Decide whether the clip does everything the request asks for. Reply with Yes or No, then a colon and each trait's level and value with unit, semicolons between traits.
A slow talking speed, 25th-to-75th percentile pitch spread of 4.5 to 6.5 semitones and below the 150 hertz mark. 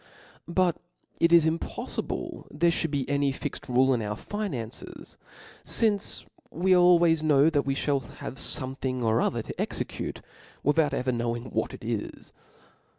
No: average, 150 wpm; average, 4.8 semitones; medium, 140 Hz